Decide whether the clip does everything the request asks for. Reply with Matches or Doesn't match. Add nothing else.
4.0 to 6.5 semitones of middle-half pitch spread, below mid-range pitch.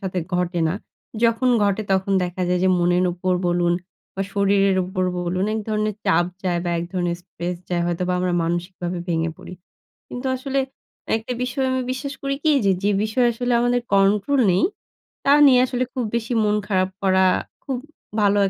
Doesn't match